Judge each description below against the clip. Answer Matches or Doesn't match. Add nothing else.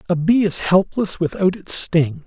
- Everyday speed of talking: Matches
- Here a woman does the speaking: Doesn't match